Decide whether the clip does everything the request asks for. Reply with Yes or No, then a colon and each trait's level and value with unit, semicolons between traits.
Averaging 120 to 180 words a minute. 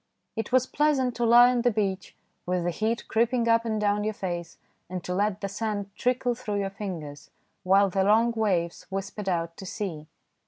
No: average, 195 wpm